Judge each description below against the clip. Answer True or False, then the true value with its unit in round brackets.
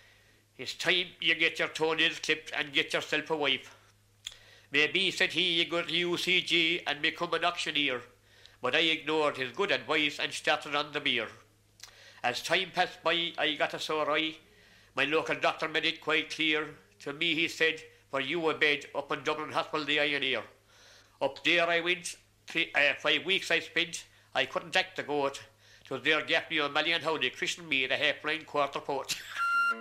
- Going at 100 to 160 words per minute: False (185 wpm)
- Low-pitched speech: False (155 Hz)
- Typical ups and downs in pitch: True (3.6 semitones)